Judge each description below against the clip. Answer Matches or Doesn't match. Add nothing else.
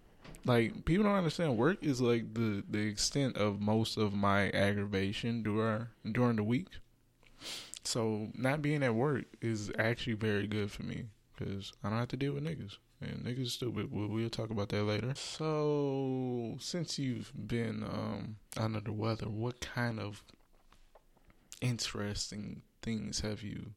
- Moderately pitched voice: Doesn't match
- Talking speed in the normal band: Matches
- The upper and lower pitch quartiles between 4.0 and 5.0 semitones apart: Doesn't match